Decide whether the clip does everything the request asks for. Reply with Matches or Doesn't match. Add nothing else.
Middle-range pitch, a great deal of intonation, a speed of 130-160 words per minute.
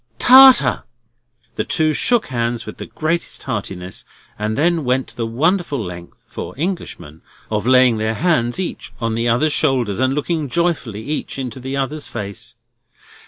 Doesn't match